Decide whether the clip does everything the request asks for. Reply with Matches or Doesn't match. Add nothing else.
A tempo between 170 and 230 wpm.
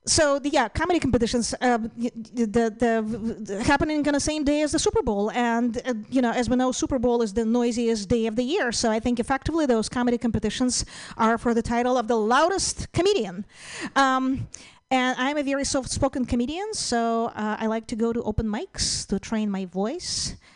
Matches